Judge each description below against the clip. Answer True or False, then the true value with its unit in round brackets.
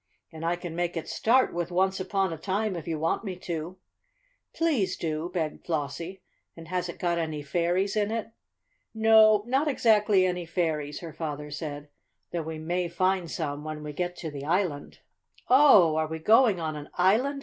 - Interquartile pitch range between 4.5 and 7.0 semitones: False (3.6 semitones)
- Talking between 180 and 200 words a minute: True (185 wpm)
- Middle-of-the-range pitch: True (175 Hz)